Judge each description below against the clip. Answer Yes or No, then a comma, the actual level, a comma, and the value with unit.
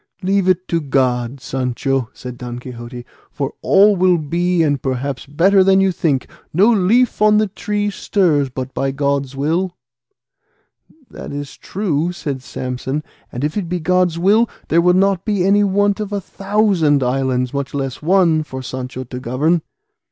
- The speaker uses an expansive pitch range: Yes, wide, 6.3 semitones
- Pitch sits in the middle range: Yes, medium, 155 Hz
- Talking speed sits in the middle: Yes, average, 165 wpm